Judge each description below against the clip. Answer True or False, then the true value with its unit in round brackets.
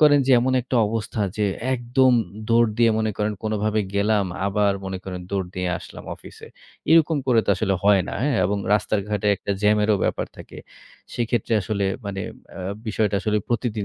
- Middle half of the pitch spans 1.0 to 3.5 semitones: True (2.7 semitones)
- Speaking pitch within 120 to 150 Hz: False (105 Hz)